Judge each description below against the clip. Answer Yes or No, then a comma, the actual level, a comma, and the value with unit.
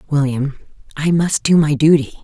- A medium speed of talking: Yes, average, 160 wpm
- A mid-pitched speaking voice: Yes, medium, 150 Hz